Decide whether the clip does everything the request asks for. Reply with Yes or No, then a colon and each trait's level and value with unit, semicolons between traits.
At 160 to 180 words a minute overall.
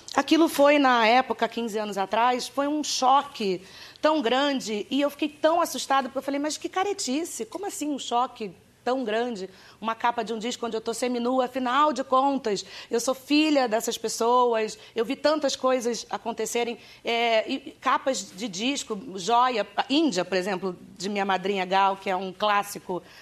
Yes: average, 175 wpm